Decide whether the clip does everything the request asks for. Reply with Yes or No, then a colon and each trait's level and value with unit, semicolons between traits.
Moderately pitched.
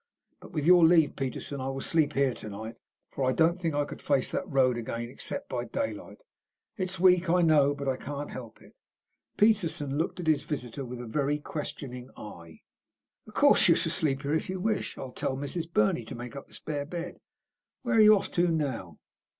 Yes: medium, 145 Hz